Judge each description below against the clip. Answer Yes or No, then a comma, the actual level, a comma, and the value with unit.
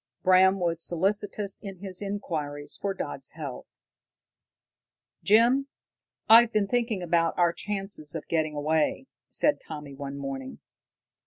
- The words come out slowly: Yes, slow, 120 wpm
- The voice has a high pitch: No, medium, 180 Hz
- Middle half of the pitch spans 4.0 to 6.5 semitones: Yes, average, 5.2 semitones